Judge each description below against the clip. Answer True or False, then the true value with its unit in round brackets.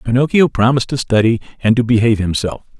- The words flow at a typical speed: True (170 wpm)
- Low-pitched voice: True (120 Hz)